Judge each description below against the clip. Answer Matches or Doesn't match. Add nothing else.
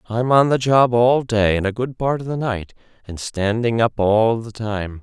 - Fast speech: Matches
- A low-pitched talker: Matches